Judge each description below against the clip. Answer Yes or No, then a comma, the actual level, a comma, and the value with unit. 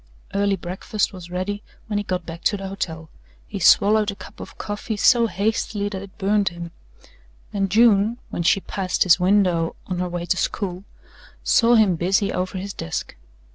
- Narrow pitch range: Yes, narrow, 2.3 semitones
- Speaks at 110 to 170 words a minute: No, average, 180 wpm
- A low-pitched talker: No, high, 195 Hz